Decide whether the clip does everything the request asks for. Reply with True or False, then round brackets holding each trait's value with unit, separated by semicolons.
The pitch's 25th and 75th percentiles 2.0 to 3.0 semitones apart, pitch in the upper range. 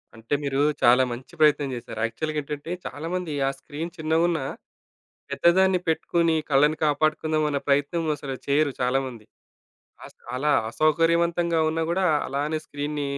False (2.7 semitones; 150 Hz)